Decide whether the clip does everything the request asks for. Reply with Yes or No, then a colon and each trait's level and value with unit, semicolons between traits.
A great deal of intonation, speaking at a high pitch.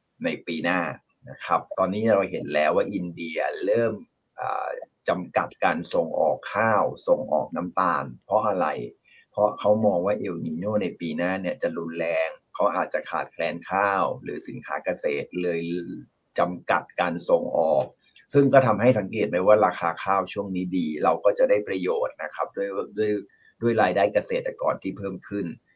No: wide, 6.5 semitones; low, 100 Hz